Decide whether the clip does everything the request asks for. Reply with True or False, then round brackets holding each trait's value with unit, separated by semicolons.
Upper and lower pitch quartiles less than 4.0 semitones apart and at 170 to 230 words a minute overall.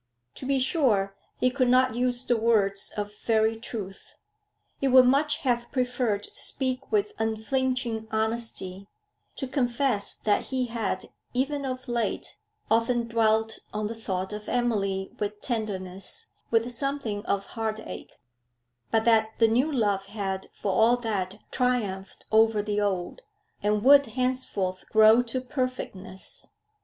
False (3.4 semitones; 140 wpm)